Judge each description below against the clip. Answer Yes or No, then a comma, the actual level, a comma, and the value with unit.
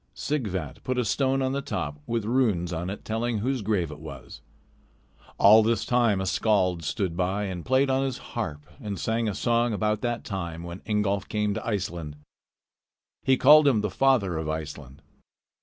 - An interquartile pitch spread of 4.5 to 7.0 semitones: Yes, average, 5.3 semitones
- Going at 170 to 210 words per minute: Yes, average, 180 wpm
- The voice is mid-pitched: No, low, 105 Hz